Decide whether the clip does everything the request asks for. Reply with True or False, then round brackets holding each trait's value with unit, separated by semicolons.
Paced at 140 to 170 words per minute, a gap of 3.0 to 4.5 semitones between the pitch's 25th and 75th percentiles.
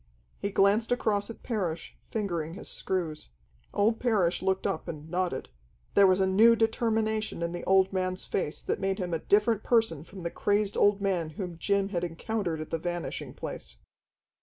False (180 wpm; 3.6 semitones)